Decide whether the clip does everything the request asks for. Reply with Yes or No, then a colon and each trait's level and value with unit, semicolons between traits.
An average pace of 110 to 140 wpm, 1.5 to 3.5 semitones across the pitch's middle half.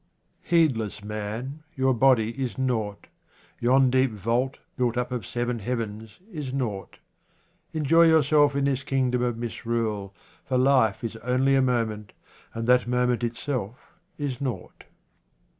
Yes: slow, 135 wpm; average, 2.8 semitones